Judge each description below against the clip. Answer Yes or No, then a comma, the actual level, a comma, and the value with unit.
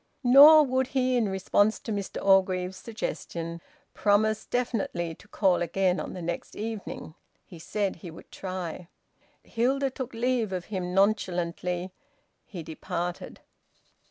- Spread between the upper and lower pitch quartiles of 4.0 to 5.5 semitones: Yes, average, 4.4 semitones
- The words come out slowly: Yes, slow, 130 wpm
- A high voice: Yes, high, 195 Hz